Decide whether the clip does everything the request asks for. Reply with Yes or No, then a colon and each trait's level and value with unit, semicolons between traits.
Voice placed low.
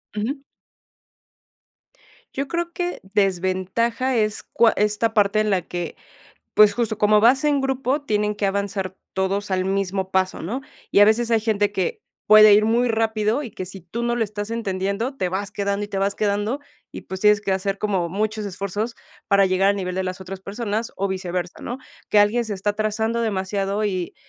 No: high, 205 Hz